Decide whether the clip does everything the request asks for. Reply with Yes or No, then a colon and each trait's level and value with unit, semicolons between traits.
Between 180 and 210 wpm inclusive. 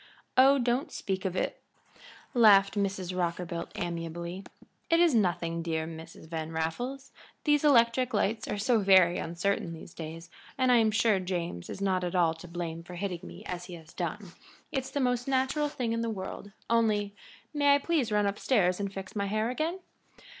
Yes: average, 185 wpm